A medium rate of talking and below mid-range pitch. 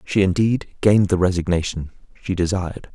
Yes: average, 145 wpm; very low, 95 Hz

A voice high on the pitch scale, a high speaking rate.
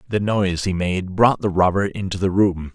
No: very low, 95 Hz; fast, 220 wpm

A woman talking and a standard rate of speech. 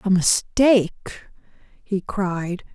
No: female; slow, 90 wpm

